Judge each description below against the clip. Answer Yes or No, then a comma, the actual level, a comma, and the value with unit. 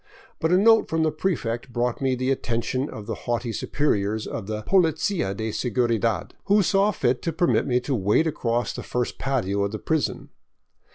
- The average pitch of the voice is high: No, low, 125 Hz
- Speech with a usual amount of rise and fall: No, wide, 5.9 semitones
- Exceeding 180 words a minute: Yes, average, 190 wpm